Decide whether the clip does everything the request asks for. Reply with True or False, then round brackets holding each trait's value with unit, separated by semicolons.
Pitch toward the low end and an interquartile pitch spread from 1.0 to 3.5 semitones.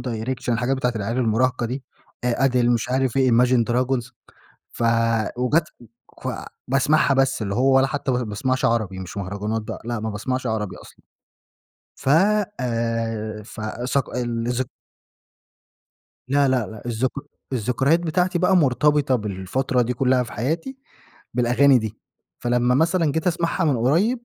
True (125 Hz; 2.8 semitones)